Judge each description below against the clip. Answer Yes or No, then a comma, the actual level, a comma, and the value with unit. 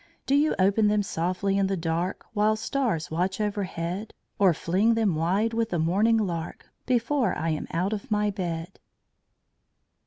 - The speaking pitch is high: Yes, high, 195 Hz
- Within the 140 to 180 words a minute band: Yes, average, 160 wpm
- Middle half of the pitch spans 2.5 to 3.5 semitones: No, average, 4.1 semitones